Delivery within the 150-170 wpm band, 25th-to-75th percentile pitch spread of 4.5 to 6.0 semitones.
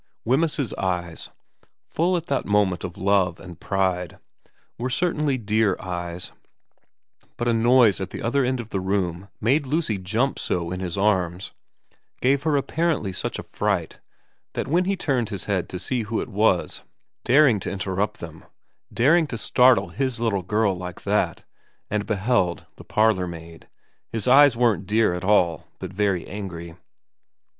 Yes: average, 160 wpm; wide, 5.5 semitones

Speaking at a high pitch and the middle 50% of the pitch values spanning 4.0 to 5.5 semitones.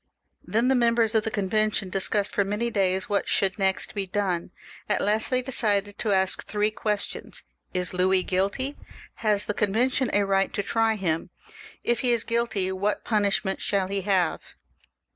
No: high, 205 Hz; narrow, 2.5 semitones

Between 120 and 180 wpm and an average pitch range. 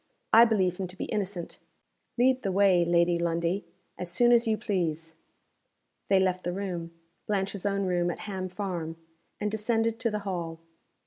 Yes: average, 170 wpm; average, 3.2 semitones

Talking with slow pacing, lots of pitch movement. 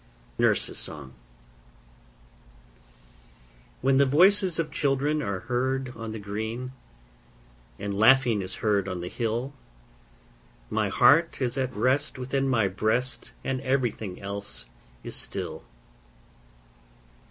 No: slow, 105 wpm; average, 4.7 semitones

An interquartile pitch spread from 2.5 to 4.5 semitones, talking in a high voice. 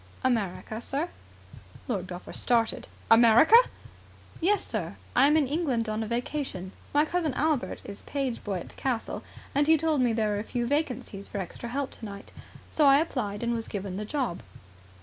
No: average, 5.2 semitones; high, 240 Hz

